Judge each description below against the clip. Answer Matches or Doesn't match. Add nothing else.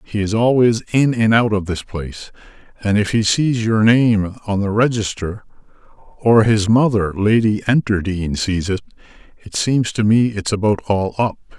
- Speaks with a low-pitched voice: Matches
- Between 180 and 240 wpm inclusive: Doesn't match